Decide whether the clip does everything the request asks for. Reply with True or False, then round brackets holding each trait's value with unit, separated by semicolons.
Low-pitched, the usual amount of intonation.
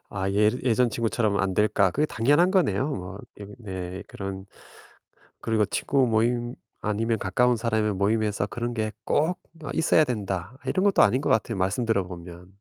True (110 Hz; 3.8 semitones)